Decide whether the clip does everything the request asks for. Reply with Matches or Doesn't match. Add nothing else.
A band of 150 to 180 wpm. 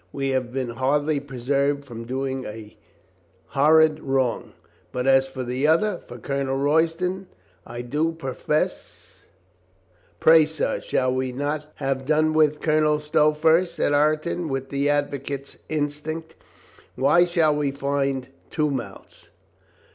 Doesn't match